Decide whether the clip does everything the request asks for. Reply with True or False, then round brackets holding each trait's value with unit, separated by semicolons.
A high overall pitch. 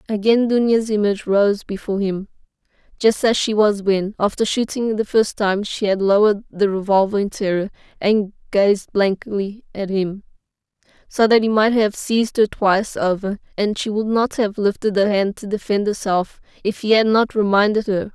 True (205 Hz)